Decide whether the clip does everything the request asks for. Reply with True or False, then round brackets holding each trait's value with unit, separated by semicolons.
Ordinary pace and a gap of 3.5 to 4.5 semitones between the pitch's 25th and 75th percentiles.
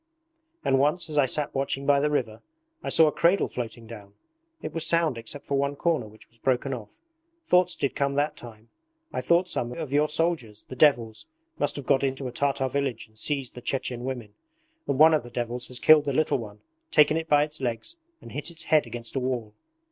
False (220 wpm; 3.9 semitones)